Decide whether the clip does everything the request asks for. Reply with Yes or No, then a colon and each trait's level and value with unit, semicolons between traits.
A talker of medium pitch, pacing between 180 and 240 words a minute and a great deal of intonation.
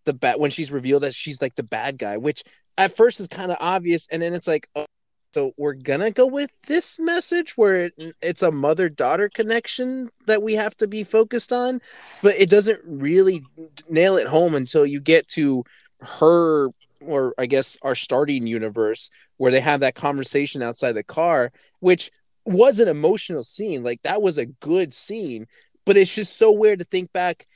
Yes: medium, 170 Hz; average, 190 wpm; wide, 7.1 semitones